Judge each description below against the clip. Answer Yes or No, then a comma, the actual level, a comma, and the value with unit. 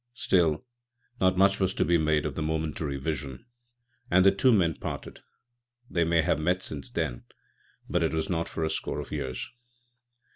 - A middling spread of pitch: Yes, average, 3.2 semitones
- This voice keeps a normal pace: Yes, average, 180 wpm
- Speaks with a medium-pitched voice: No, very low, 80 Hz